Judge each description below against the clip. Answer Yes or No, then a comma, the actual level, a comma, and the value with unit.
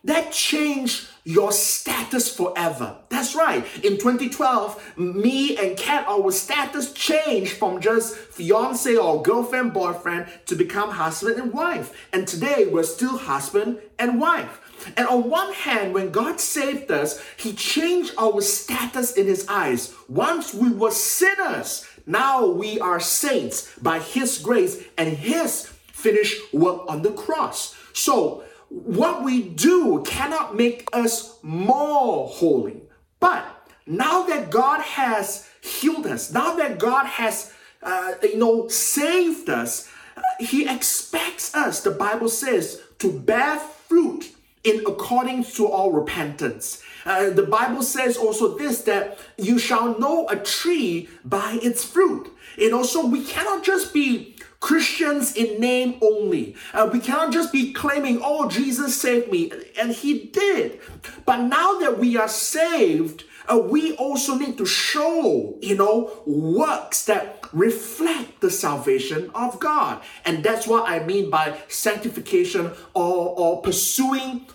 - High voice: Yes, very high, 250 Hz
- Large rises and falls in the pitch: Yes, wide, 7.2 semitones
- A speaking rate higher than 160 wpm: No, average, 140 wpm